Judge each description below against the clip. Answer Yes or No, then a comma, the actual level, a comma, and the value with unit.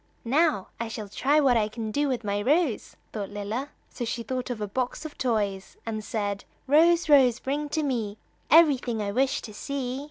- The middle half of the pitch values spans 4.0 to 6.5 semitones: Yes, average, 4.8 semitones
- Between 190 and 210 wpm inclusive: Yes, average, 195 wpm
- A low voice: No, high, 245 Hz